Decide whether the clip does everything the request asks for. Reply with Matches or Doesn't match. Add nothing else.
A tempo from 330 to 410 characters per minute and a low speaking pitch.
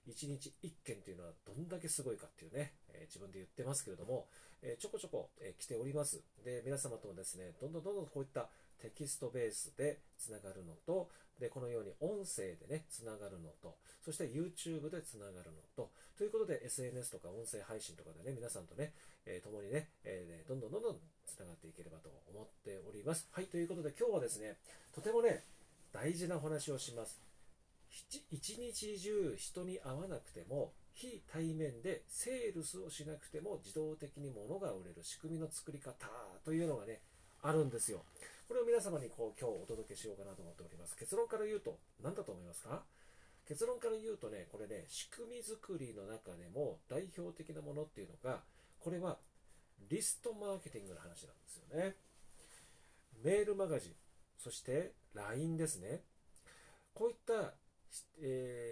Doesn't match